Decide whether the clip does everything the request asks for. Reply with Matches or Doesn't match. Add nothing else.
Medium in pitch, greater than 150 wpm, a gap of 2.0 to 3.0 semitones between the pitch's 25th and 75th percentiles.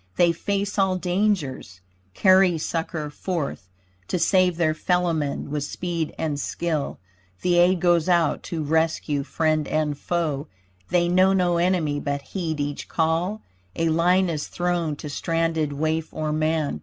Doesn't match